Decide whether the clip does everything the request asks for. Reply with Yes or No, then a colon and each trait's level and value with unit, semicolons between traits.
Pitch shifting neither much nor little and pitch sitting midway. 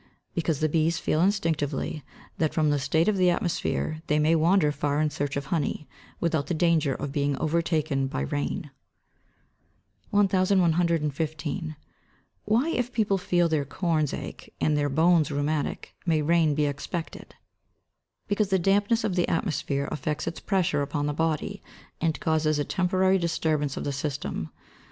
Yes: average, 3.2 semitones; medium, 155 Hz